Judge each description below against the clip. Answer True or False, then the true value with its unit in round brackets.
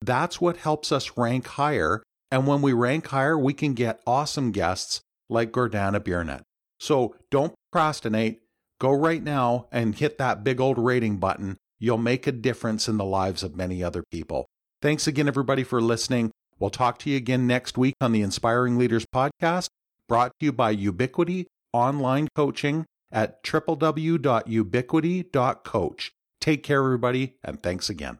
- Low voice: True (125 Hz)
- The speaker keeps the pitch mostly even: False (4.4 semitones)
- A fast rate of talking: False (160 wpm)